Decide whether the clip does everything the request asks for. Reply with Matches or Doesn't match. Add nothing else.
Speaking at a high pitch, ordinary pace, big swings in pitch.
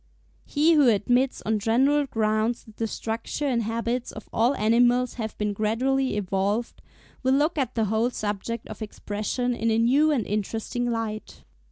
Doesn't match